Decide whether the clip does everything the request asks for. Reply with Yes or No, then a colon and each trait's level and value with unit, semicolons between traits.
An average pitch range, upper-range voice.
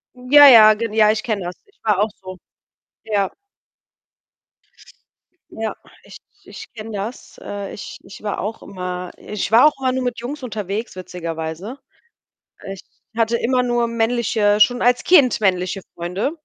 Yes: average, 3.7 semitones; high, 215 Hz